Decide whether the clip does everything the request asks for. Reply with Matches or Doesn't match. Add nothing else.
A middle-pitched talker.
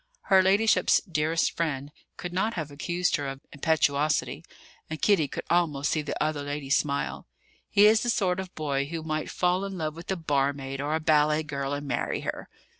Matches